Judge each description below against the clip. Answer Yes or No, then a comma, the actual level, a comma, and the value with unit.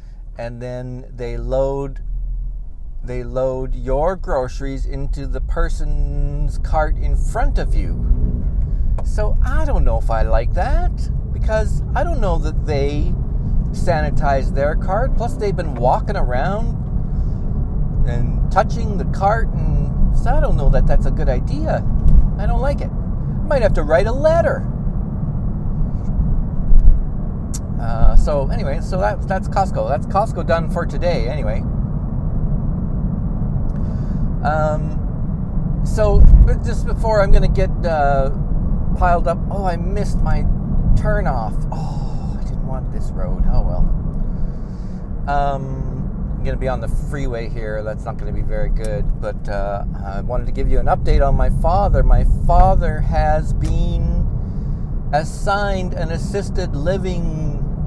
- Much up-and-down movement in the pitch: Yes, wide, 5.7 semitones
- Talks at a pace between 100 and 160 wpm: Yes, average, 140 wpm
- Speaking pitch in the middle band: No, low, 130 Hz